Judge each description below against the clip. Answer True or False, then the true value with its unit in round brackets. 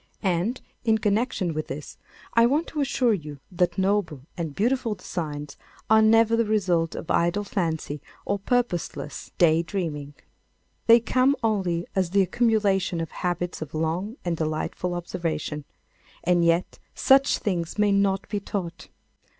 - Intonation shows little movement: False (4.6 semitones)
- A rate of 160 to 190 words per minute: False (145 wpm)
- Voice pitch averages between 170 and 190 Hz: True (185 Hz)